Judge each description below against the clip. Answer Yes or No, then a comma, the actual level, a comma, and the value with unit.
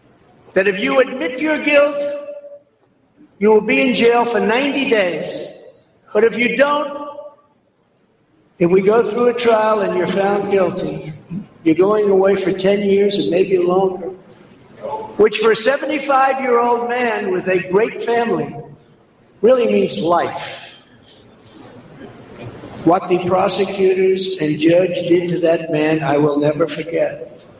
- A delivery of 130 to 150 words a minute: Yes, average, 140 wpm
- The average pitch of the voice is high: Yes, high, 205 Hz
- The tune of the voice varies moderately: No, wide, 6.5 semitones